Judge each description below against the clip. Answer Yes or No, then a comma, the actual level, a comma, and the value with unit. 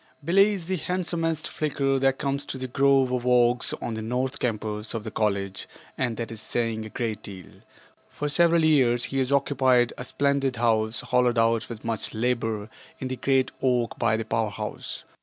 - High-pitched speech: No, low, 125 Hz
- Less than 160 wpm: No, average, 190 wpm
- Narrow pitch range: No, average, 3.4 semitones